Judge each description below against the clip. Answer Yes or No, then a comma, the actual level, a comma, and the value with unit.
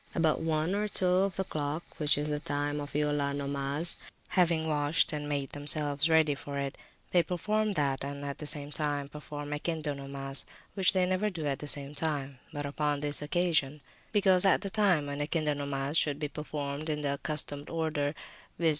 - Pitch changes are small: Yes, narrow, 2.3 semitones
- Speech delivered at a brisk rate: No, average, 190 wpm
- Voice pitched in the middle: Yes, medium, 150 Hz